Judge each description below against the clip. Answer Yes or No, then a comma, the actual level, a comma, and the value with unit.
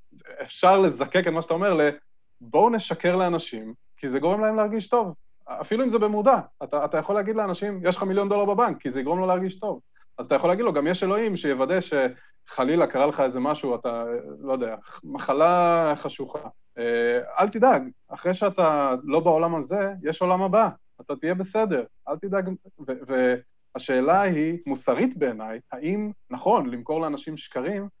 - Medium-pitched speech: Yes, medium, 175 Hz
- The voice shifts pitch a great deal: Yes, wide, 6.0 semitones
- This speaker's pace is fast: Yes, fast, 170 wpm